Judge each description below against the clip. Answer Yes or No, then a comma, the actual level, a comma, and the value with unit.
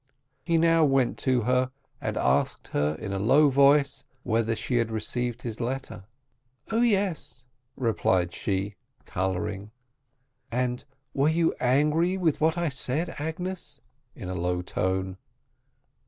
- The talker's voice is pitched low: Yes, low, 125 Hz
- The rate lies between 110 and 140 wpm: Yes, slow, 135 wpm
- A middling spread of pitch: No, wide, 7.0 semitones